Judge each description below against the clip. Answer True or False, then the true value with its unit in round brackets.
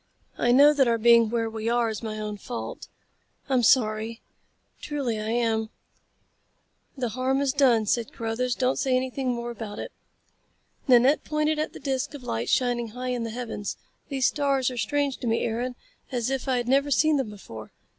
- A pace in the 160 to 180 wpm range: False (190 wpm)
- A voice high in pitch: True (245 Hz)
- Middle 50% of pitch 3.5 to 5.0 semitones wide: False (3.0 semitones)